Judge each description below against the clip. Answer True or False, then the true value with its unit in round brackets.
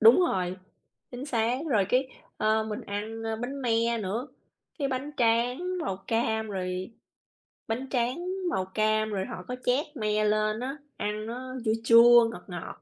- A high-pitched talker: True (225 Hz)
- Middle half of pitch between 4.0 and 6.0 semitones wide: False (2.8 semitones)